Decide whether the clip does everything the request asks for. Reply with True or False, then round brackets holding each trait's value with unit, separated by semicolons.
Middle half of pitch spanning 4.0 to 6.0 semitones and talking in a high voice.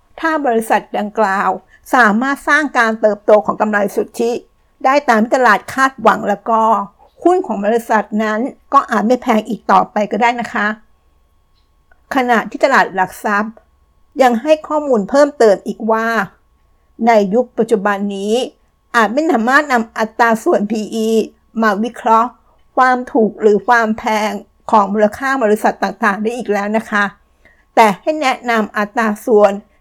False (2.8 semitones; 225 Hz)